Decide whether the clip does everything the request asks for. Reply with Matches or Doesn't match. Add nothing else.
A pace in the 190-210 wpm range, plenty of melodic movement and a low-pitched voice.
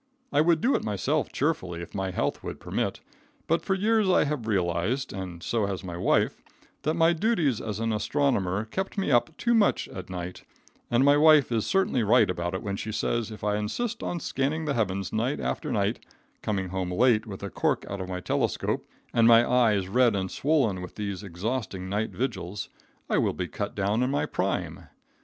Matches